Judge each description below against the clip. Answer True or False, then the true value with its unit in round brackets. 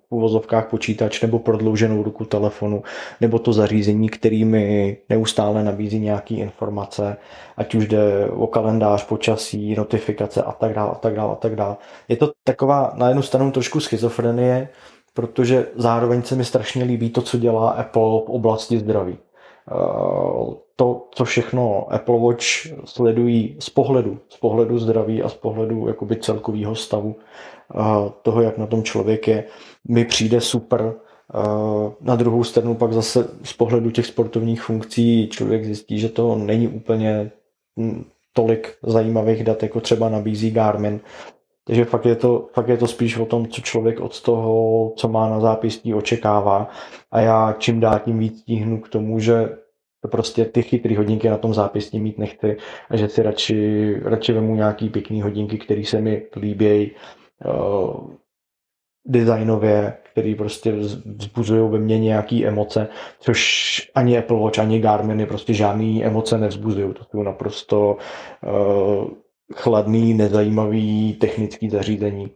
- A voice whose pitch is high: False (110 Hz)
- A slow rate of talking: False (145 wpm)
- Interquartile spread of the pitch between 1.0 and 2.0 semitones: True (1.7 semitones)